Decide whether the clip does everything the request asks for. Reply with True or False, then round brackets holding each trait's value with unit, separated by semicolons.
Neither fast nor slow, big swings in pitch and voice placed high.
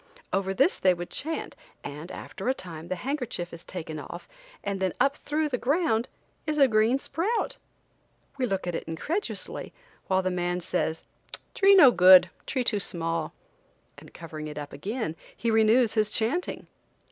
True (170 wpm; 7.0 semitones; 200 Hz)